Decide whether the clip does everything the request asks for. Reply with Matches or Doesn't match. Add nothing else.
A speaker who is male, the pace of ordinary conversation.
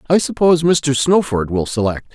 Matches